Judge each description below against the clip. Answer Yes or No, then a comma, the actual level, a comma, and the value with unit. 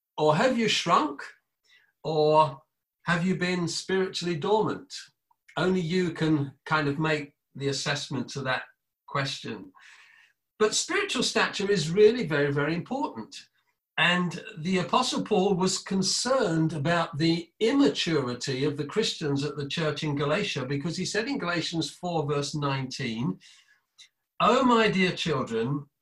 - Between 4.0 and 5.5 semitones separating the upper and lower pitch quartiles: Yes, average, 4.7 semitones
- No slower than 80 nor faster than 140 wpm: Yes, slow, 135 wpm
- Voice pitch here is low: No, medium, 165 Hz